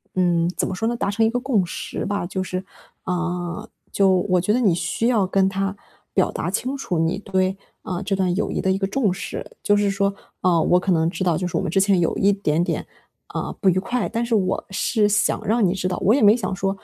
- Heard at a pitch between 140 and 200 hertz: Yes, high, 195 Hz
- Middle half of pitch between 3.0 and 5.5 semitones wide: No, narrow, 2.5 semitones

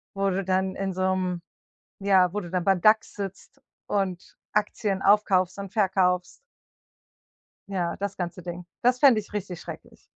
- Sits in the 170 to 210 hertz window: Yes, high, 190 Hz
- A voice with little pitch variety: Yes, narrow, 1.8 semitones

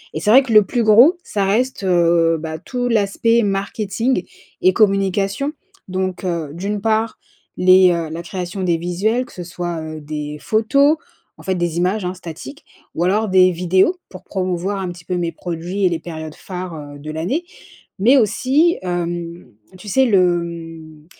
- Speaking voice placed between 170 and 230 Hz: Yes, medium, 185 Hz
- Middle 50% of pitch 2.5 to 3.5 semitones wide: No, average, 4.0 semitones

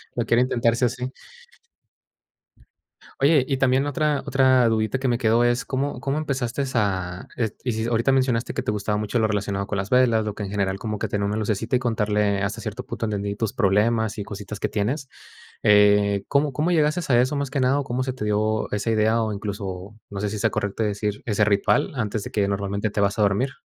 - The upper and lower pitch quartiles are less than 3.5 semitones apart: No, average, 3.8 semitones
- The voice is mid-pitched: No, low, 110 Hz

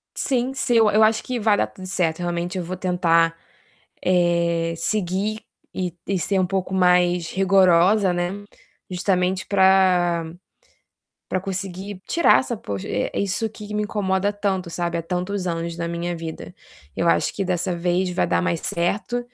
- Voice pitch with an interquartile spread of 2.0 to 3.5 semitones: Yes, narrow, 2.5 semitones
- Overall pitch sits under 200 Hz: Yes, medium, 185 Hz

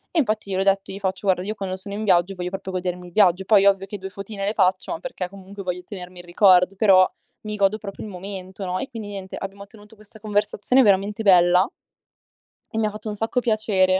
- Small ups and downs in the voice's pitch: Yes, narrow, 2.1 semitones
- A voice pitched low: No, high, 195 Hz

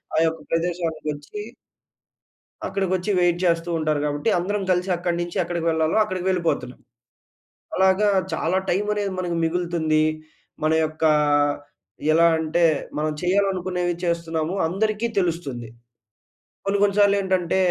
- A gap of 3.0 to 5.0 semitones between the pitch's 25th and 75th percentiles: No, narrow, 2.6 semitones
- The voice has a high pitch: No, medium, 175 Hz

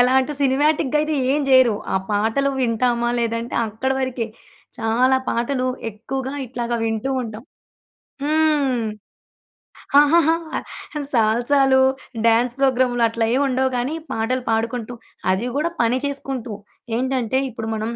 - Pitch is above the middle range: Yes, very high, 250 Hz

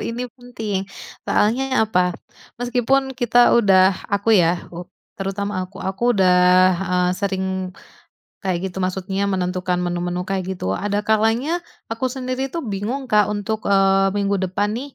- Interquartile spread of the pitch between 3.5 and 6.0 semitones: Yes, average, 4.1 semitones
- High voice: Yes, high, 200 Hz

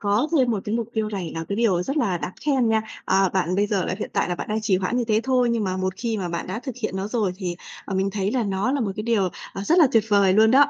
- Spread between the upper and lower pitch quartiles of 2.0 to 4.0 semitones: Yes, average, 3.6 semitones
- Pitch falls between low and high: No, high, 210 Hz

